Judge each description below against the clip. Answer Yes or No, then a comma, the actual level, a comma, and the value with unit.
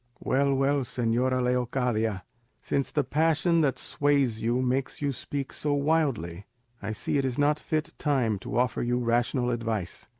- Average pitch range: Yes, average, 3.3 semitones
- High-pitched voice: No, low, 130 Hz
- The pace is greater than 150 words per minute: Yes, average, 165 wpm